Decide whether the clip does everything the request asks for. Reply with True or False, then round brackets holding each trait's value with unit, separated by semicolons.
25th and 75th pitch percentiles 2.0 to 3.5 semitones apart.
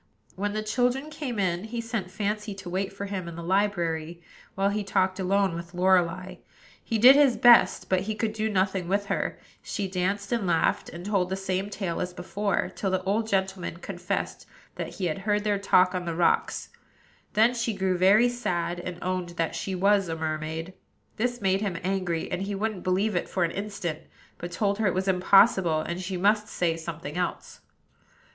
True (2.7 semitones)